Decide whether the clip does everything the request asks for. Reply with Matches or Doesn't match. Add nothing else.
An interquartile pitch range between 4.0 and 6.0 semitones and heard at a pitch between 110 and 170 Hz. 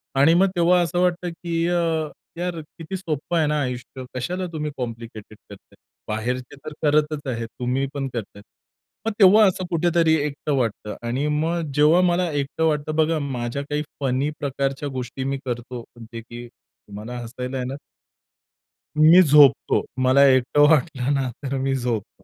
Matches